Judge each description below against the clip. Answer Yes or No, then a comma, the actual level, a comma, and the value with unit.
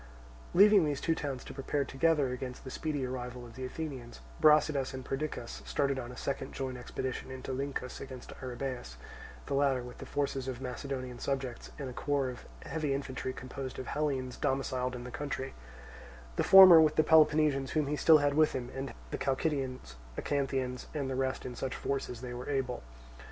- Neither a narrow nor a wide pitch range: No, narrow, 2.2 semitones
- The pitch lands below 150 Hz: Yes, low, 135 Hz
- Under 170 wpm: No, average, 190 wpm